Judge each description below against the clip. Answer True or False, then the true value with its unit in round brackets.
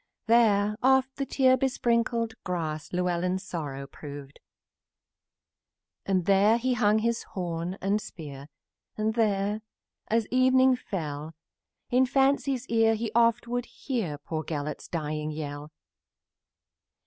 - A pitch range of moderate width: False (6.8 semitones)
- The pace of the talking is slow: True (115 wpm)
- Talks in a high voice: True (210 Hz)